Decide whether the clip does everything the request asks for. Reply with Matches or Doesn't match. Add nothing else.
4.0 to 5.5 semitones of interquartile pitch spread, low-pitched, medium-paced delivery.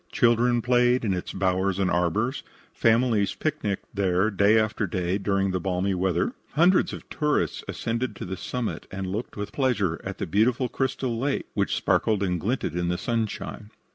Matches